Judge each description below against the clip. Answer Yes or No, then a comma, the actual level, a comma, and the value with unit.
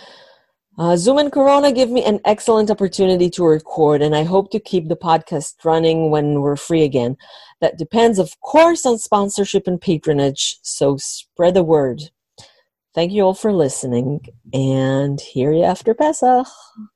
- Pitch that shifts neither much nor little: No, wide, 6.1 semitones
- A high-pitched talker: No, medium, 175 Hz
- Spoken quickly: Yes, fast, 160 wpm